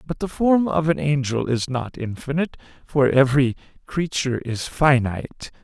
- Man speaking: Yes, male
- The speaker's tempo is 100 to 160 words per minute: Yes, average, 150 wpm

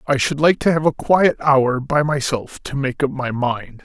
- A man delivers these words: Yes, male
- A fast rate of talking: Yes, fast, 235 wpm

